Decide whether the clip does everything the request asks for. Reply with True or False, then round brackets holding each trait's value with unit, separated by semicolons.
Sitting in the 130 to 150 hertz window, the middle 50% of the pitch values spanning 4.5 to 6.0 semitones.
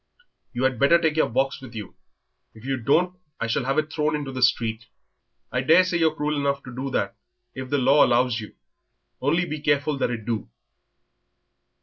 False (135 Hz; 3.5 semitones)